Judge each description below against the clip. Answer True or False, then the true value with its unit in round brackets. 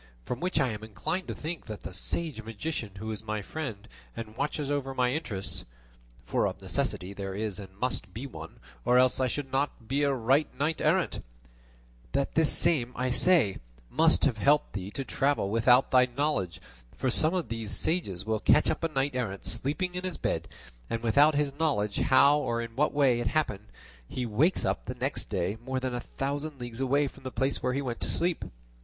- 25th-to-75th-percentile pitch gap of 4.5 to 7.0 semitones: True (4.8 semitones)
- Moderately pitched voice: False (130 Hz)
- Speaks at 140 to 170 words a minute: False (205 wpm)